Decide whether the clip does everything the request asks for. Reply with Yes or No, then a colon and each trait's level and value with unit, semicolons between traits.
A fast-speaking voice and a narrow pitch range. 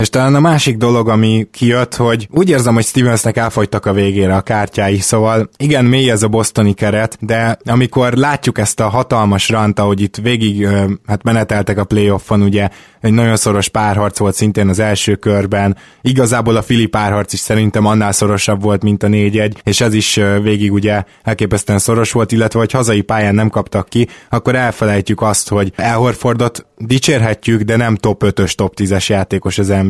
Yes: fast, 180 wpm; narrow, 2.2 semitones